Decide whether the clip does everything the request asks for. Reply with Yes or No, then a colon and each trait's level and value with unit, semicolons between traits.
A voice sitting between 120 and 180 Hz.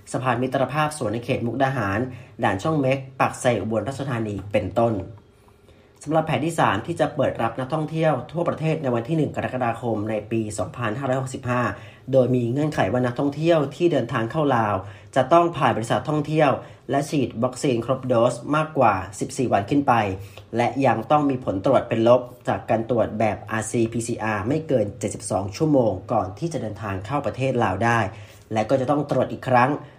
Yes: low, 125 Hz